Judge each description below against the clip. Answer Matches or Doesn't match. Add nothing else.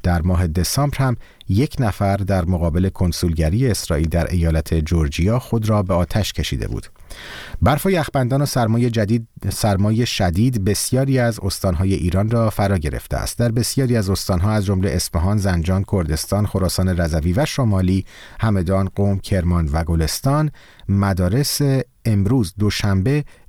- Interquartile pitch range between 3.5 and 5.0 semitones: Matches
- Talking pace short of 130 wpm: Doesn't match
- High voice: Doesn't match